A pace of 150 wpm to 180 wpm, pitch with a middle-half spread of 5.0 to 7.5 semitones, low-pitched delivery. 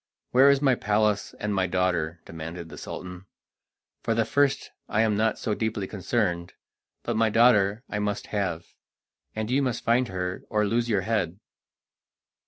No: average, 165 wpm; average, 3.7 semitones; low, 105 Hz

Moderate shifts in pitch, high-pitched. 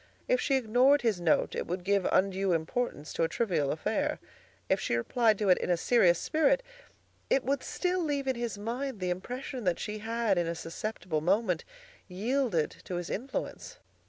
No: wide, 6.1 semitones; high, 210 Hz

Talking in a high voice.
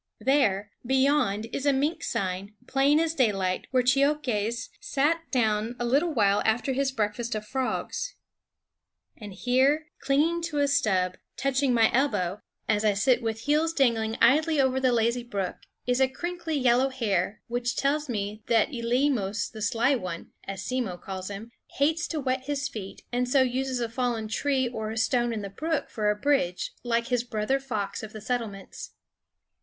Yes: high, 245 Hz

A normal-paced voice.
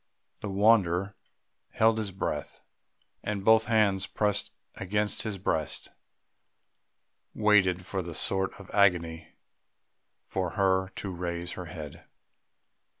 No: slow, 110 wpm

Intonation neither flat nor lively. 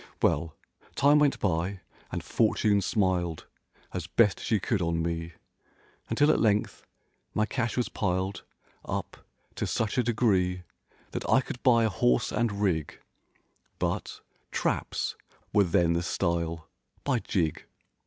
Yes: average, 5.0 semitones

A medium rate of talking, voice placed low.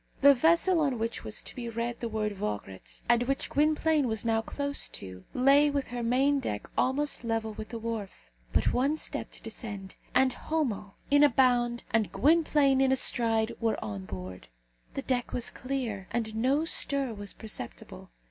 No: average, 180 wpm; high, 240 Hz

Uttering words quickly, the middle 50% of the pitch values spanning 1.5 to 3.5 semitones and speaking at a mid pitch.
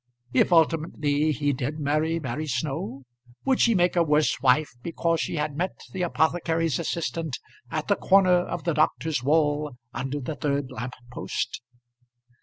No: average, 155 wpm; average, 2.7 semitones; medium, 155 Hz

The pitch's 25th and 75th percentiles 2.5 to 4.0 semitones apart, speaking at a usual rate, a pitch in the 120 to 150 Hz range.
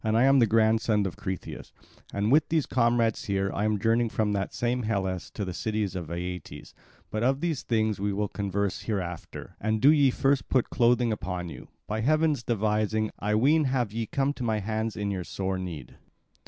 No: average, 3.3 semitones; average, 195 wpm; low, 110 Hz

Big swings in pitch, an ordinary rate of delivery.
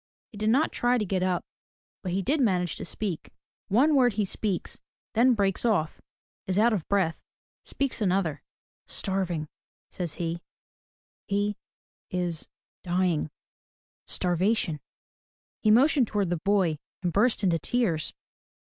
No: average, 3.9 semitones; average, 165 wpm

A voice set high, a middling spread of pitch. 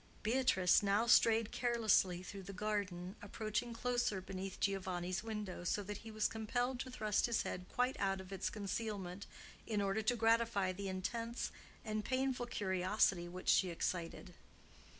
Yes: high, 205 Hz; average, 3.5 semitones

